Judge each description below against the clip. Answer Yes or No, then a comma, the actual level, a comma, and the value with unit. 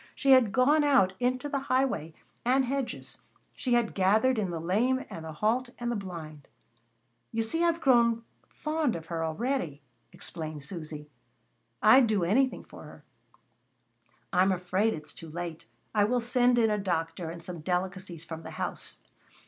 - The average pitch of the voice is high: Yes, high, 205 Hz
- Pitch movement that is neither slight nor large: No, wide, 7.3 semitones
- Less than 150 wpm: No, average, 165 wpm